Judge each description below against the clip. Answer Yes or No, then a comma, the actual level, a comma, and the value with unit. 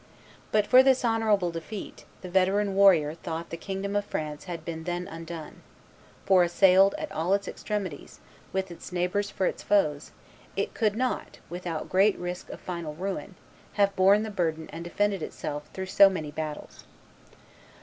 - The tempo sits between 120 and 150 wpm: No, average, 165 wpm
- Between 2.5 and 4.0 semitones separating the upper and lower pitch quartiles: Yes, average, 3.3 semitones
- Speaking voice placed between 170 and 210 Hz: Yes, medium, 185 Hz